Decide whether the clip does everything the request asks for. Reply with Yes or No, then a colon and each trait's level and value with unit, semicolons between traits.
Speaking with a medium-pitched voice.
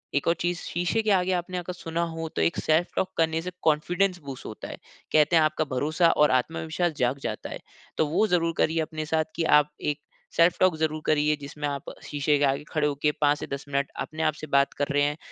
Yes: medium, 155 Hz